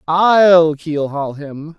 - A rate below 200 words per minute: Yes, slow, 135 wpm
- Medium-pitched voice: Yes, medium, 160 Hz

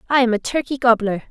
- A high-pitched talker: Yes, high, 240 Hz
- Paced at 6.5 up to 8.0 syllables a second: Yes, 6.7 syllables/s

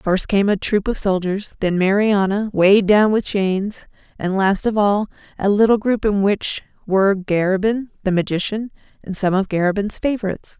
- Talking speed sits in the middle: Yes, average, 170 wpm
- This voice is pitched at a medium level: No, high, 200 Hz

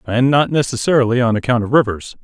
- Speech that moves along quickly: No, average, 190 wpm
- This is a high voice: No, low, 125 Hz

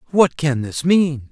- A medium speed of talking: Yes, average, 180 wpm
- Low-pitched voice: No, medium, 145 Hz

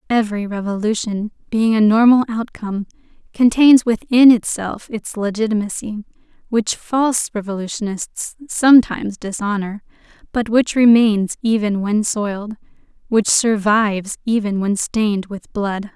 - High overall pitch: Yes, high, 215 Hz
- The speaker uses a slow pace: Yes, slow, 110 wpm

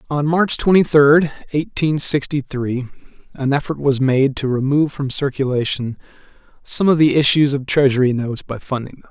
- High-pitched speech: No, medium, 140 Hz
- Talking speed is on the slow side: No, average, 165 wpm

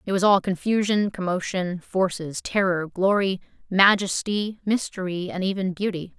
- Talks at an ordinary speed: No, slow, 125 wpm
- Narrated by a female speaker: Yes, female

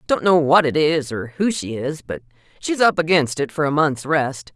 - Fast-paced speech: Yes, fast, 235 wpm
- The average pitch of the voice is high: No, medium, 150 Hz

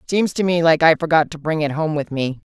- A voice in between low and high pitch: Yes, medium, 160 Hz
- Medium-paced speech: No, fast, 290 wpm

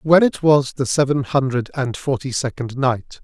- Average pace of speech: Yes, average, 185 wpm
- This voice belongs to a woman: No, male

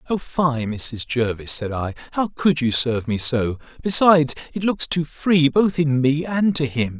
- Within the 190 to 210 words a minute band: Yes, average, 195 wpm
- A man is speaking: Yes, male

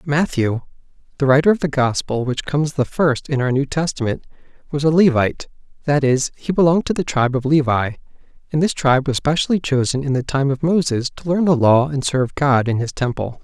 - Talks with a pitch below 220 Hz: Yes, medium, 140 Hz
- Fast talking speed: Yes, fast, 210 wpm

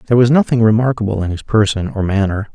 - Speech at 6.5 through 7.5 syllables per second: Yes, 6.9 syllables/s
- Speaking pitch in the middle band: No, low, 110 Hz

